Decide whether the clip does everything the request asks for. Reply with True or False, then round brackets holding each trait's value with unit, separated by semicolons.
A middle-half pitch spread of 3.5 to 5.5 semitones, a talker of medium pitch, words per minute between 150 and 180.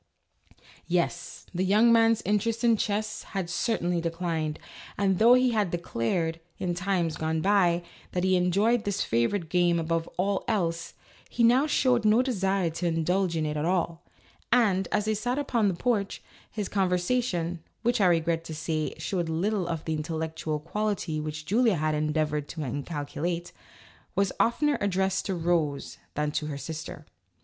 True (4.3 semitones; 180 Hz; 165 wpm)